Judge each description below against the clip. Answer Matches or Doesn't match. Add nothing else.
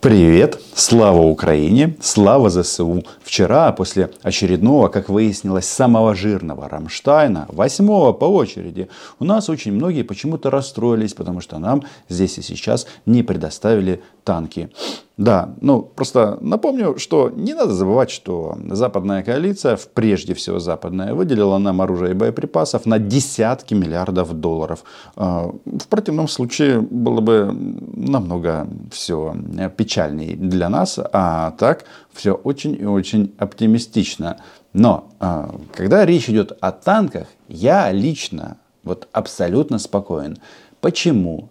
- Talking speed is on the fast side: Doesn't match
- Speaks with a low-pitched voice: Matches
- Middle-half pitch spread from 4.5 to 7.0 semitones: Matches